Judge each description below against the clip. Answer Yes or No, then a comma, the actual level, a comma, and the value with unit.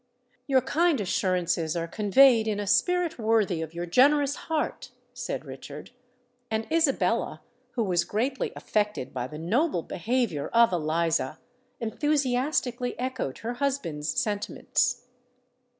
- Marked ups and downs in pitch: Yes, wide, 7.2 semitones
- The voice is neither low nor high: No, high, 225 Hz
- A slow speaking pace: Yes, slow, 120 wpm